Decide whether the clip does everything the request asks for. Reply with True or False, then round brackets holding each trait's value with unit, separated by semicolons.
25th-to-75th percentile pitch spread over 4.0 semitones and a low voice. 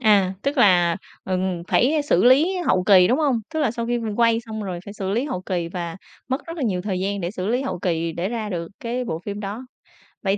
False (4.8 semitones; 205 Hz)